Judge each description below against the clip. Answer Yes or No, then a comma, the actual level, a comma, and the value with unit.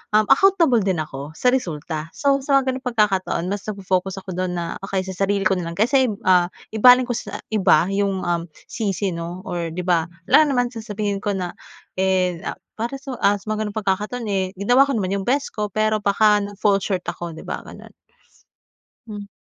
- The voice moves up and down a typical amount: Yes, average, 3.5 semitones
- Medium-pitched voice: No, high, 200 Hz